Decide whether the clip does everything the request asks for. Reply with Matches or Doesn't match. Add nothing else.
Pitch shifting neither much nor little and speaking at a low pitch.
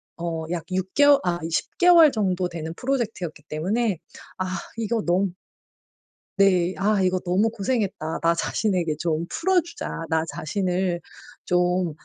Doesn't match